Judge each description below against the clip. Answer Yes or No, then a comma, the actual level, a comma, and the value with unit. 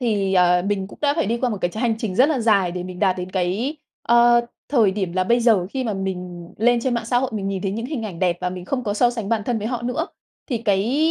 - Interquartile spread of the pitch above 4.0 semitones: Yes, average, 4.5 semitones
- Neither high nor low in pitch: No, high, 215 Hz